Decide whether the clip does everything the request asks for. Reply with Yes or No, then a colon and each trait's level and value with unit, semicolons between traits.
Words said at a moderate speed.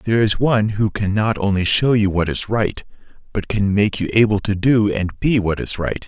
No: fast, 235 wpm